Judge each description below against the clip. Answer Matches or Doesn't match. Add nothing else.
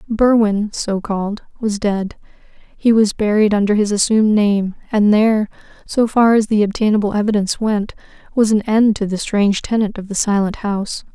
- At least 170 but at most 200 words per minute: Doesn't match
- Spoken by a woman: Matches